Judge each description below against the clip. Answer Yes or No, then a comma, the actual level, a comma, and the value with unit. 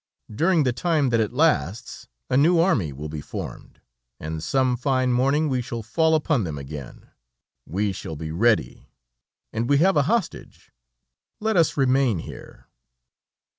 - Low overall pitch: Yes, low, 125 Hz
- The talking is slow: No, average, 155 wpm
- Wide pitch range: Yes, wide, 8.6 semitones